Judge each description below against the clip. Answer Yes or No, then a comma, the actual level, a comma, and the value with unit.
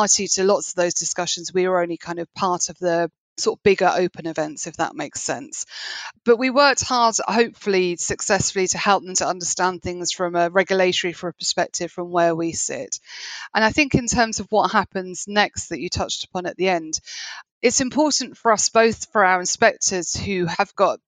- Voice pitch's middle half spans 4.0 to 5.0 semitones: No, average, 3.1 semitones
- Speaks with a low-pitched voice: No, medium, 185 Hz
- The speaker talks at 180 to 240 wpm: Yes, average, 200 wpm